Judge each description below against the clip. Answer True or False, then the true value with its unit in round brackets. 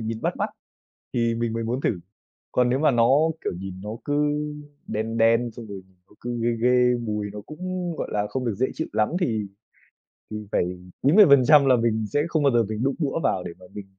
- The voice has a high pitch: False (120 Hz)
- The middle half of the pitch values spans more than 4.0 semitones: False (3.7 semitones)